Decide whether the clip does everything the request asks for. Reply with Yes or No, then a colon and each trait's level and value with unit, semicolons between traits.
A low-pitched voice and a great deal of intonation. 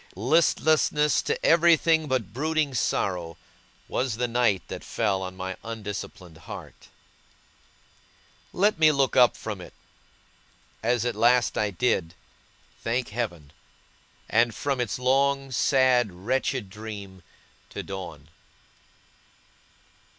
Yes: low, 120 Hz; wide, 5.8 semitones